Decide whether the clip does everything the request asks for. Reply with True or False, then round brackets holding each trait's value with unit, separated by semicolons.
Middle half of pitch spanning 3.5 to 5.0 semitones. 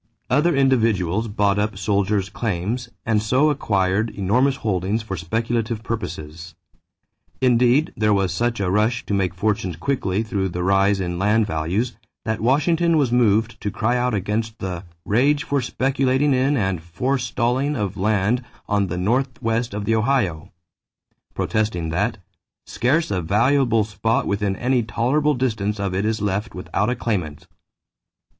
True (4.1 semitones)